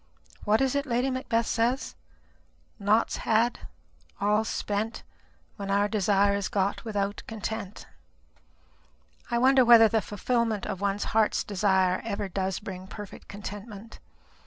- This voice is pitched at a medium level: No, high, 210 Hz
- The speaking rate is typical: No, slow, 130 wpm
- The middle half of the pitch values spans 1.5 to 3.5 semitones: Yes, narrow, 2.4 semitones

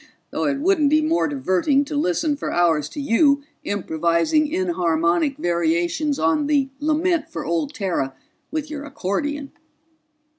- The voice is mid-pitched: No, very high, 285 Hz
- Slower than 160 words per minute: Yes, average, 140 wpm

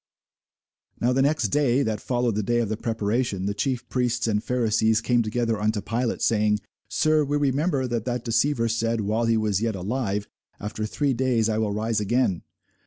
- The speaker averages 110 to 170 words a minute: No, average, 185 wpm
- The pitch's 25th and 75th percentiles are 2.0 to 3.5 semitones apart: Yes, average, 2.8 semitones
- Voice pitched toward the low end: Yes, low, 115 Hz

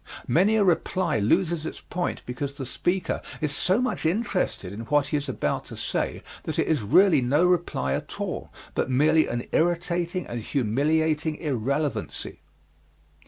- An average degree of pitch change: Yes, average, 4.9 semitones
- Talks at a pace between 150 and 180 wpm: Yes, average, 160 wpm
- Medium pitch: Yes, medium, 155 Hz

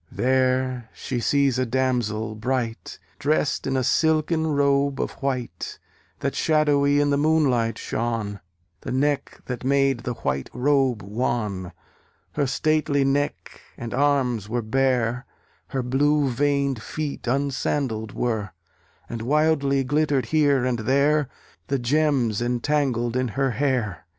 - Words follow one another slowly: Yes, slow, 130 wpm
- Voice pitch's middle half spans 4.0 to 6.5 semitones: No, average, 3.1 semitones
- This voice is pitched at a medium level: No, low, 130 Hz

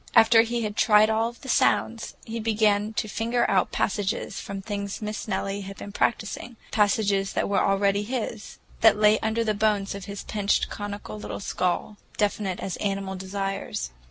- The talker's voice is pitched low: No, high, 205 Hz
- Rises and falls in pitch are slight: Yes, narrow, 1.8 semitones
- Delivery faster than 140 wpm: Yes, average, 175 wpm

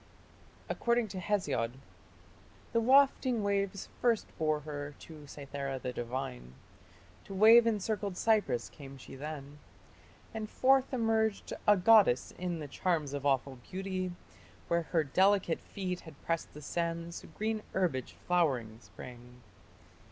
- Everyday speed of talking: No, slow, 130 wpm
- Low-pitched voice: No, medium, 170 Hz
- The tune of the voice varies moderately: No, wide, 6.9 semitones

